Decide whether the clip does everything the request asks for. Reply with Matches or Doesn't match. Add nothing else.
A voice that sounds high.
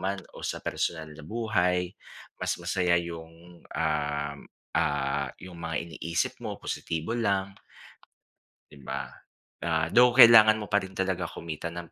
Doesn't match